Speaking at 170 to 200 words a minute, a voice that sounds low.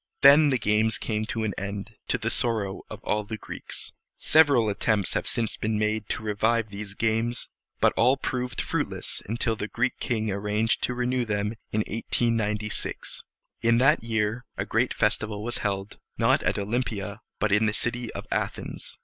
Yes: average, 175 wpm; low, 110 Hz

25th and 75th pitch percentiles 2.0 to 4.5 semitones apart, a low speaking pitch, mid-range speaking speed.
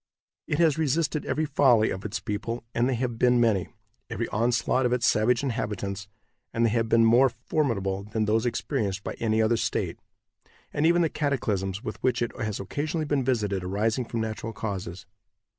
Yes: average, 3.8 semitones; low, 115 Hz; average, 180 wpm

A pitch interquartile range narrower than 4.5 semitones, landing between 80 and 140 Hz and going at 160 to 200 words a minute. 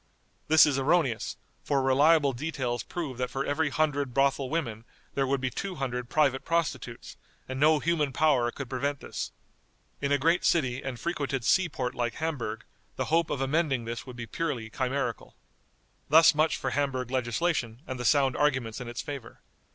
Yes: average, 3.5 semitones; low, 135 Hz; average, 175 wpm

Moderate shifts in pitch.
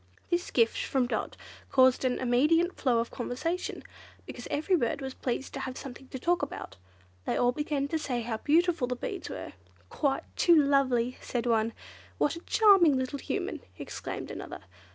Yes: average, 4.4 semitones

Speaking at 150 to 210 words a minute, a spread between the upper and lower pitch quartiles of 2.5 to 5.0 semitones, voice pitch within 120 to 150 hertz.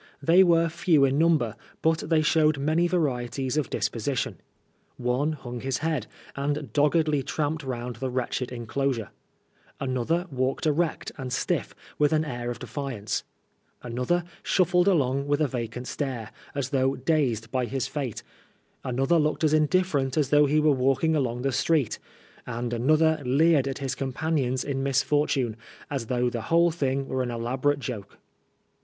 Yes: average, 160 wpm; average, 3.7 semitones; medium, 140 Hz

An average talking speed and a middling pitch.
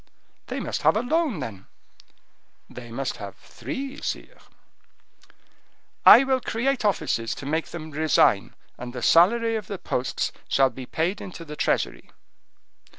Yes: average, 145 wpm; medium, 160 Hz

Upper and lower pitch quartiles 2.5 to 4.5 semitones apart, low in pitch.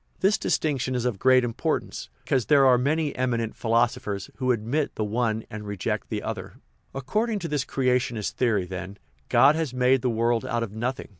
Yes: average, 3.1 semitones; low, 125 Hz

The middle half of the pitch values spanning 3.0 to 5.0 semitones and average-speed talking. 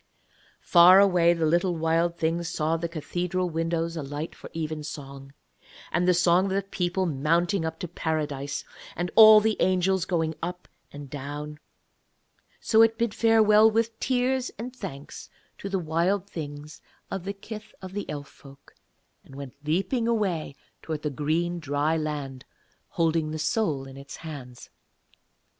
Yes: average, 4.1 semitones; average, 150 wpm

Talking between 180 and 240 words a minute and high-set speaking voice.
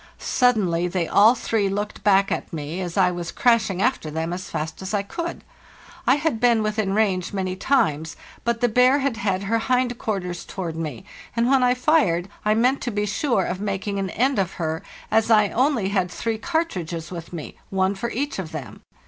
Yes: average, 200 wpm; high, 200 Hz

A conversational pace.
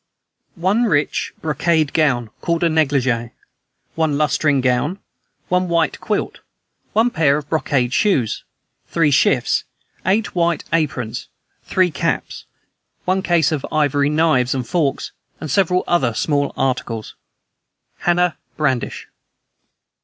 No: slow, 115 wpm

